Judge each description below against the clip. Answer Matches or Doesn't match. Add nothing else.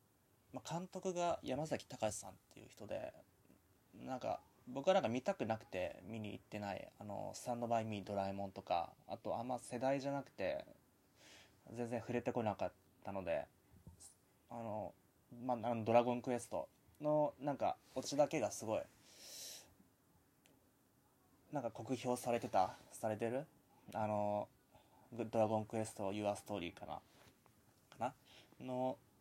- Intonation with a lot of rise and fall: Doesn't match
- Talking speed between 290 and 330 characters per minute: Doesn't match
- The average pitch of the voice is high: Doesn't match